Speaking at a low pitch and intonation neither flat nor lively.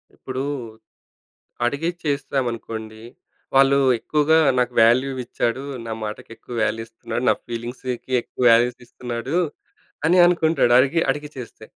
Yes: low, 125 Hz; average, 3.0 semitones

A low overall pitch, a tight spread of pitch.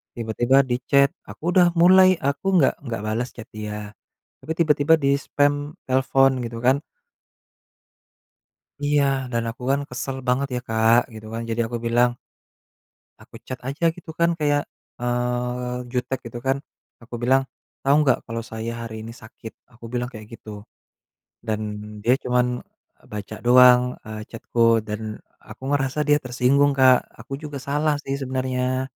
No: low, 125 Hz; average, 3.2 semitones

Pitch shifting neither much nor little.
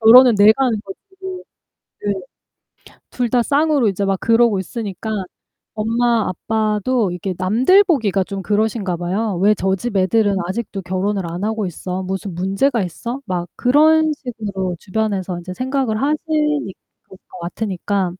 Yes: average, 4.4 semitones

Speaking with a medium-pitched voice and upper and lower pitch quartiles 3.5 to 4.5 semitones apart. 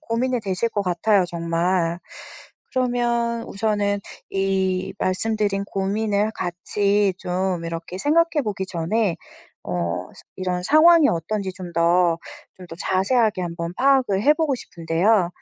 No: high, 195 Hz; average, 4.2 semitones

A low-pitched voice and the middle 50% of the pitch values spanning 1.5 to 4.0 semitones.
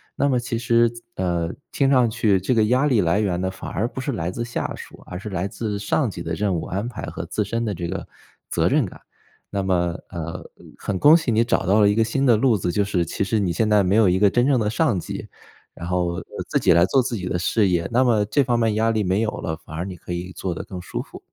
No: low, 105 Hz; average, 4.4 semitones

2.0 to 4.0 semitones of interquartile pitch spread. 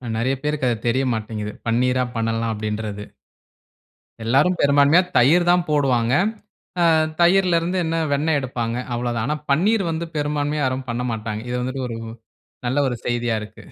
No: average, 4.6 semitones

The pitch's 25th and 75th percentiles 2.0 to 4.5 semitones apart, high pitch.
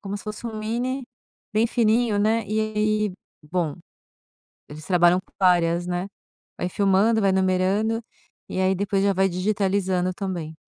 Yes: average, 2.8 semitones; high, 195 Hz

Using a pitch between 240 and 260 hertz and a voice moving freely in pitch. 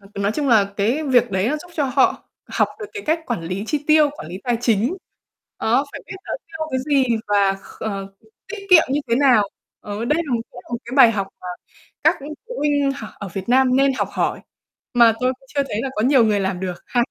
Yes: high, 245 Hz; wide, 5.9 semitones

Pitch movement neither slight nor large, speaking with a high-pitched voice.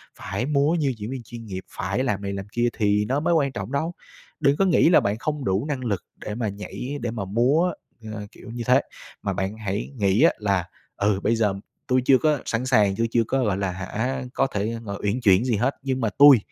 No: average, 4.8 semitones; low, 115 Hz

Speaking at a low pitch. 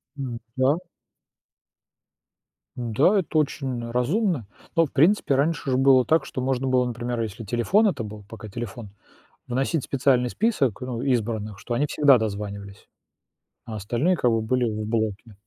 Yes: low, 125 Hz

